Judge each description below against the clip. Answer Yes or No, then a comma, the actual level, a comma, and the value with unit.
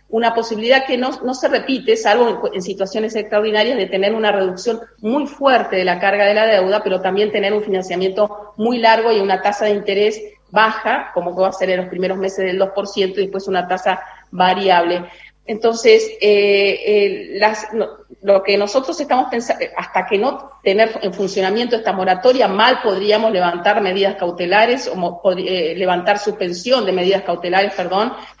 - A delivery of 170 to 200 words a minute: Yes, average, 175 wpm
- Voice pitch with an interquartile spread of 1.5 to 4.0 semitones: Yes, average, 3.1 semitones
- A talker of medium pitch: No, high, 205 Hz